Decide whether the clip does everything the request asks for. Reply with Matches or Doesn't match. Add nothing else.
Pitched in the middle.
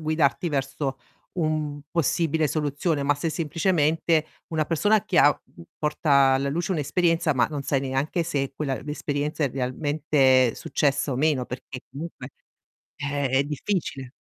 Matches